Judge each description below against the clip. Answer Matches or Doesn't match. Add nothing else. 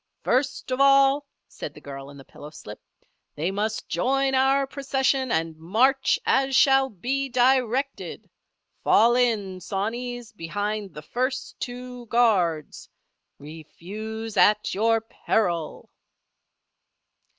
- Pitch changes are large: Matches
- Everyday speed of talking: Doesn't match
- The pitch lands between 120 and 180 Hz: Doesn't match